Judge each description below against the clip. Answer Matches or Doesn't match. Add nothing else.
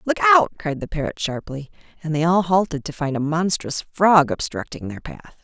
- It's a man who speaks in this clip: Doesn't match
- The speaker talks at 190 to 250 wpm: Matches